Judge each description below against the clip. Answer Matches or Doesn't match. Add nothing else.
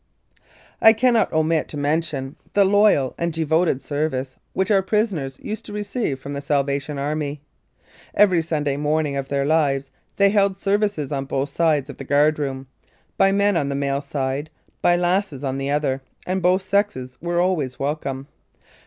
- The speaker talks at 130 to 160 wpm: Doesn't match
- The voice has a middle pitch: Matches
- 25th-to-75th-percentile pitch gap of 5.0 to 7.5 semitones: Matches